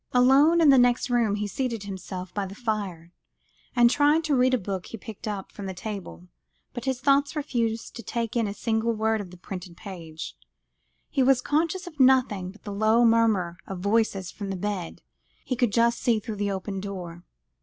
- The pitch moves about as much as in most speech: Yes, average, 4.4 semitones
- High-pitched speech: Yes, high, 220 Hz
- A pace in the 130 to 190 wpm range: No, average, 200 wpm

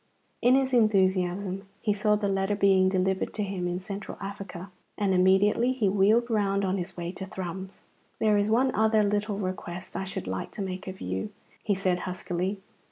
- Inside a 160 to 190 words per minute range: Yes, average, 185 wpm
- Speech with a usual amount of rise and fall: No, narrow, 2.0 semitones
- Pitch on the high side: Yes, high, 195 Hz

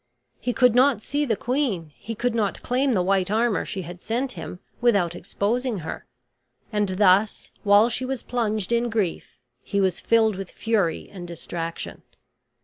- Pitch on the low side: No, high, 215 Hz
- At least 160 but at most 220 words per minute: Yes, average, 165 wpm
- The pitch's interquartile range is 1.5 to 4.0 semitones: No, average, 4.4 semitones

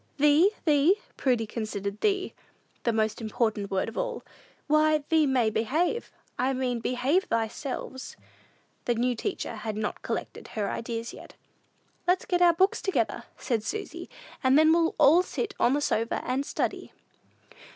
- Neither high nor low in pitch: No, very high, 260 Hz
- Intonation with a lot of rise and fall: Yes, wide, 6.2 semitones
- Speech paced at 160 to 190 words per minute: No, average, 150 wpm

